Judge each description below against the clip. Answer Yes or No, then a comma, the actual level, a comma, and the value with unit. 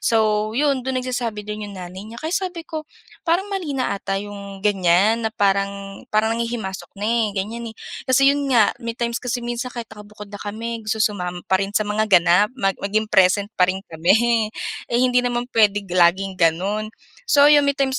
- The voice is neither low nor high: No, high, 215 Hz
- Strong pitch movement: No, average, 3.4 semitones